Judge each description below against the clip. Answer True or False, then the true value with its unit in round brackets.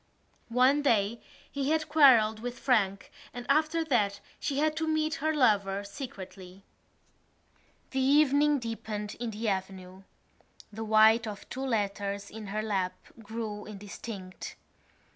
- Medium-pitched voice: False (225 Hz)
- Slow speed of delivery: True (130 wpm)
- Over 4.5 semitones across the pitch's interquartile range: True (5.3 semitones)